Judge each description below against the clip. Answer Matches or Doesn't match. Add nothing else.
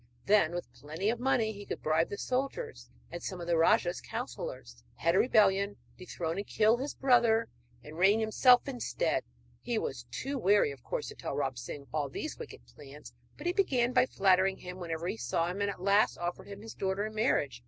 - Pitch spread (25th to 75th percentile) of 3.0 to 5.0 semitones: Doesn't match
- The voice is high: Matches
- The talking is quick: Matches